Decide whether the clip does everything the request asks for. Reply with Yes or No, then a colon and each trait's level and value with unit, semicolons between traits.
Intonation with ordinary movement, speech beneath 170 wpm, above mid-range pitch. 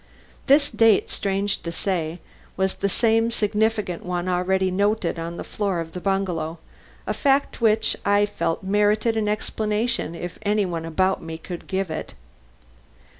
Yes: average, 3.3 semitones; average, 155 wpm; high, 195 Hz